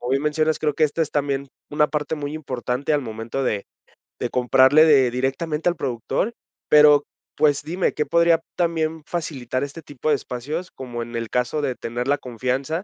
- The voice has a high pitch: No, medium, 145 Hz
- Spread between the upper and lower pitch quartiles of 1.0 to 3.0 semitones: No, average, 3.6 semitones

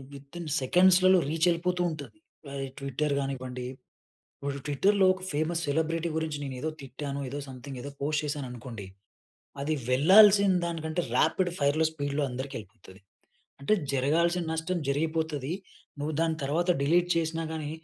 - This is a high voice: No, medium, 150 Hz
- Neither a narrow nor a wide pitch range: Yes, average, 3.4 semitones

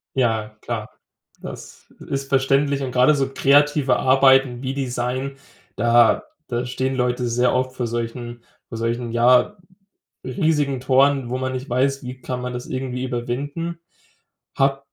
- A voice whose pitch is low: Yes, low, 130 Hz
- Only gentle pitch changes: Yes, narrow, 2.0 semitones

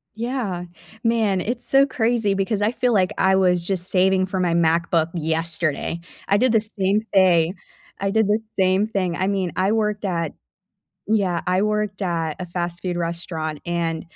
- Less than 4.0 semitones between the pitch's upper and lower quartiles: Yes, average, 3.5 semitones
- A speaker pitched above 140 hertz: Yes, medium, 185 Hz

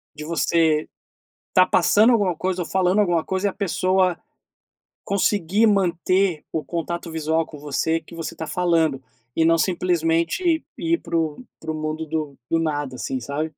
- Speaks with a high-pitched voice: No, medium, 165 Hz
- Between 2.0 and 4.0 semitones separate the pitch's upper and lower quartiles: Yes, average, 2.8 semitones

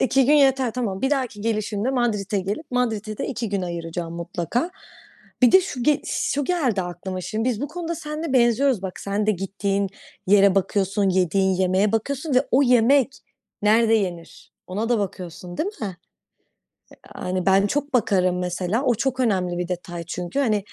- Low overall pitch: No, high, 210 Hz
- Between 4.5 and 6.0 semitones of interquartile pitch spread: Yes, wide, 5.4 semitones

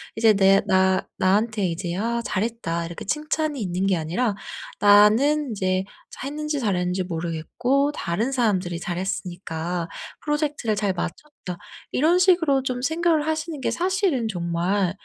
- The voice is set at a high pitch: Yes, high, 210 Hz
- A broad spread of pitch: Yes, wide, 7.7 semitones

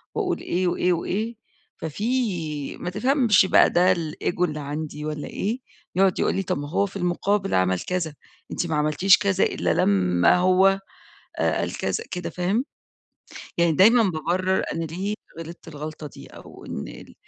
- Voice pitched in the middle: Yes, medium, 180 Hz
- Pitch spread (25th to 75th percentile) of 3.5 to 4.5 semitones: Yes, average, 4.1 semitones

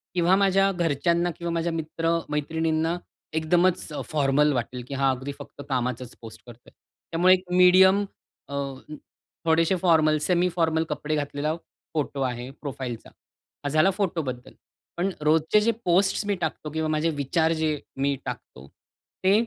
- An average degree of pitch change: Yes, average, 3.7 semitones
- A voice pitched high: No, medium, 160 Hz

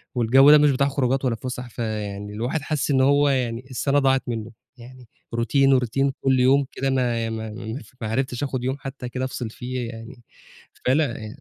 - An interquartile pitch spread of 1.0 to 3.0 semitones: Yes, average, 2.7 semitones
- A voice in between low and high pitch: No, low, 130 Hz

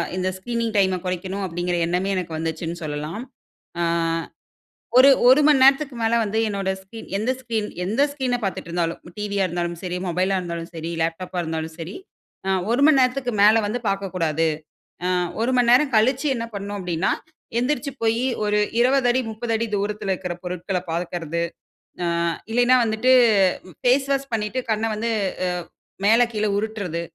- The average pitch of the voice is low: No, high, 205 Hz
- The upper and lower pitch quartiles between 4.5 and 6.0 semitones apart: Yes, average, 5.2 semitones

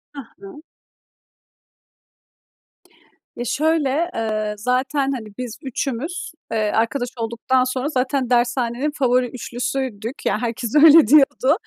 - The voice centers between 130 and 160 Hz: No, very high, 255 Hz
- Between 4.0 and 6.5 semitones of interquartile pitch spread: No, average, 3.0 semitones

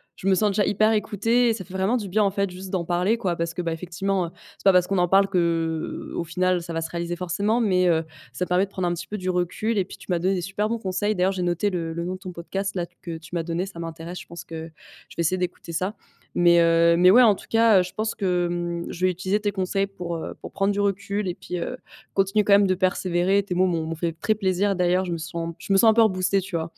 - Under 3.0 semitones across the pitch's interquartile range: Yes, narrow, 2.5 semitones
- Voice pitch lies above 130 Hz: Yes, medium, 185 Hz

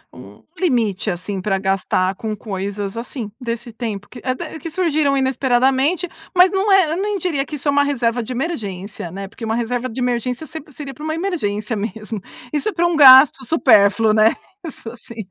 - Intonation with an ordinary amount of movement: No, wide, 6.0 semitones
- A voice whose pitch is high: Yes, high, 245 Hz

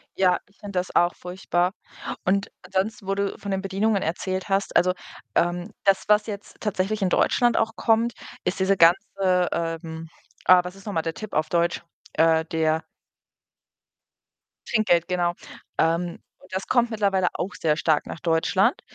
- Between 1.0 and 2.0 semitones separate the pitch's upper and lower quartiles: No, average, 2.8 semitones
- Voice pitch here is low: No, medium, 185 Hz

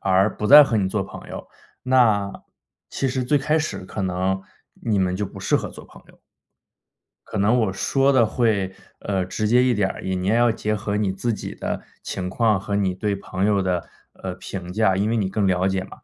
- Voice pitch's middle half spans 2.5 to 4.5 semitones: Yes, average, 3.2 semitones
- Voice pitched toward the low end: Yes, low, 100 Hz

